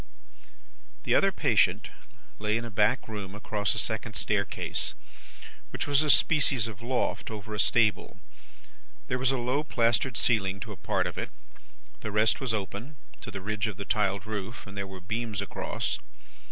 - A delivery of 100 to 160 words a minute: No, average, 175 wpm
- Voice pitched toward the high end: No, low, 110 Hz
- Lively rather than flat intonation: No, average, 2.9 semitones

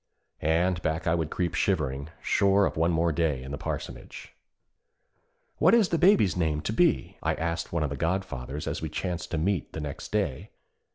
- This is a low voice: Yes, very low, 85 Hz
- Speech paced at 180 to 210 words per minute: Yes, average, 190 wpm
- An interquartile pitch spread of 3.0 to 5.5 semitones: Yes, average, 3.8 semitones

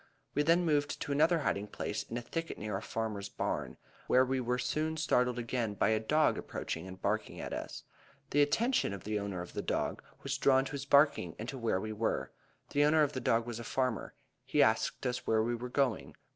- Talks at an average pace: No, fast, 225 wpm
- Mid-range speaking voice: No, low, 125 Hz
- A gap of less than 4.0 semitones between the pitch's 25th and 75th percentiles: No, average, 4.9 semitones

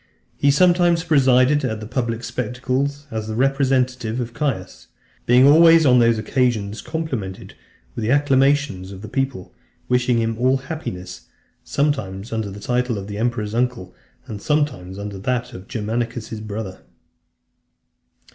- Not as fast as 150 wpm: Yes, average, 140 wpm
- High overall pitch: No, low, 125 Hz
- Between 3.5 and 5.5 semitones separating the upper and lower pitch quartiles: Yes, average, 4.1 semitones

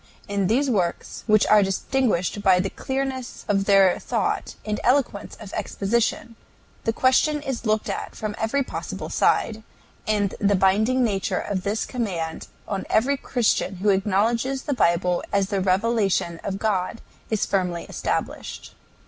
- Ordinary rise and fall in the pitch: Yes, average, 3.5 semitones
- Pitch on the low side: No, high, 210 Hz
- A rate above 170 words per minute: No, average, 150 wpm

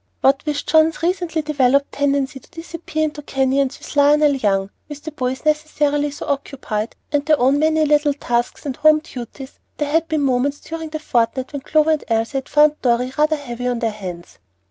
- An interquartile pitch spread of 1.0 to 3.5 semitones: Yes, average, 3.0 semitones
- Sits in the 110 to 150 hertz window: No, very high, 285 Hz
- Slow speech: No, average, 190 wpm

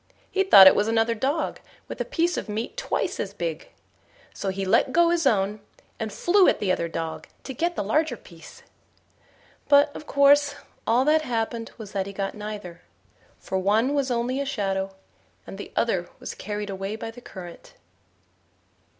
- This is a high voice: Yes, high, 225 Hz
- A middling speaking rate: Yes, average, 180 wpm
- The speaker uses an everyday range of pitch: No, wide, 6.4 semitones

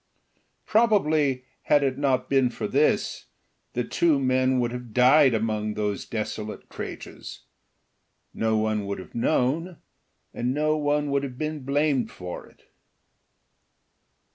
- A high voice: No, low, 130 Hz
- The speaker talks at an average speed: No, slow, 130 wpm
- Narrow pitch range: No, average, 4.5 semitones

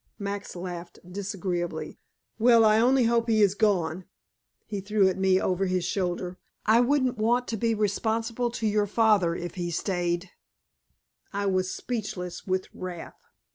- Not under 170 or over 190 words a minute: No, average, 155 wpm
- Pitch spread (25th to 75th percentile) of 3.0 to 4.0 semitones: Yes, average, 3.6 semitones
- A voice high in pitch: Yes, high, 200 Hz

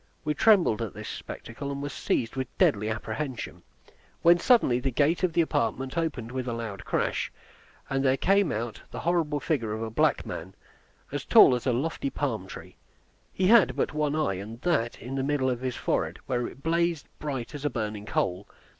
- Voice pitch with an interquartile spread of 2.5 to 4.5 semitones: No, average, 4.9 semitones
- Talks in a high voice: No, low, 135 Hz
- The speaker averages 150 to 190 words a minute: No, average, 200 wpm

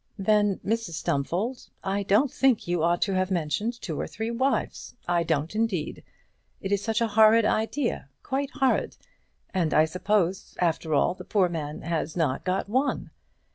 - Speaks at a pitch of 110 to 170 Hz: No, high, 195 Hz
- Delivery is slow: No, average, 170 wpm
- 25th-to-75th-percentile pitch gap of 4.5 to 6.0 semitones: Yes, average, 4.8 semitones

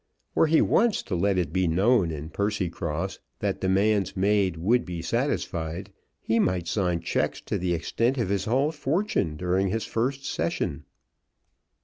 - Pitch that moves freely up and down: No, average, 4.9 semitones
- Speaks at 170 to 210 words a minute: No, average, 155 wpm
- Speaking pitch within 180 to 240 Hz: No, very low, 95 Hz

